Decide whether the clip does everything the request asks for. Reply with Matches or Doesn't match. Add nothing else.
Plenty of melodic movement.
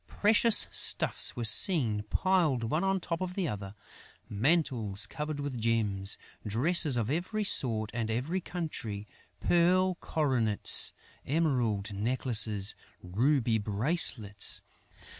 Matches